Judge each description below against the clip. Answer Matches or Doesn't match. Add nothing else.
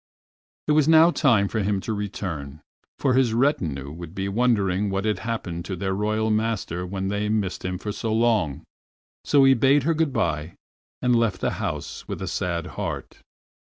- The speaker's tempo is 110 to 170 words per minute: Doesn't match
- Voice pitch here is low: Matches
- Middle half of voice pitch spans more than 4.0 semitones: Matches